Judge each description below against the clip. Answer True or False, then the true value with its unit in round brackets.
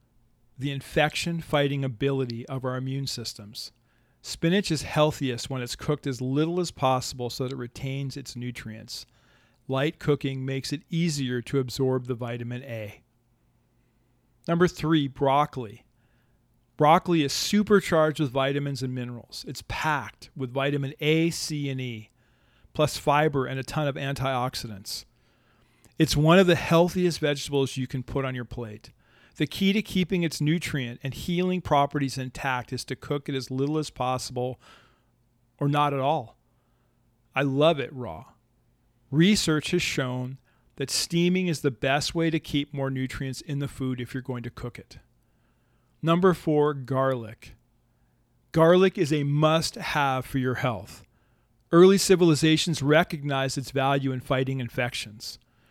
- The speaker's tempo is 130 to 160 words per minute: True (150 wpm)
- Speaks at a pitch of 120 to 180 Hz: True (135 Hz)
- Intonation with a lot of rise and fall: False (3.7 semitones)